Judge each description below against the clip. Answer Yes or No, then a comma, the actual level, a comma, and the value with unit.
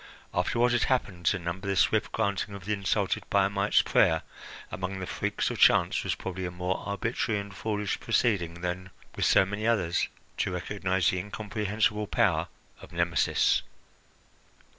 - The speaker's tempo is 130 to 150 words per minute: No, average, 160 wpm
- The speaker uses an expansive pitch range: No, average, 2.7 semitones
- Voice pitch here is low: Yes, low, 100 Hz